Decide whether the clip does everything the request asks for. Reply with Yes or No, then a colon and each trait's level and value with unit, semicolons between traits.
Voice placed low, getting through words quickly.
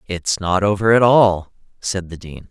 No: very low, 95 Hz; average, 190 wpm